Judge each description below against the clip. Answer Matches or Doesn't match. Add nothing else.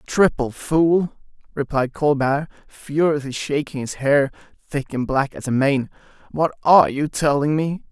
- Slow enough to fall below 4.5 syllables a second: Matches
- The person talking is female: Doesn't match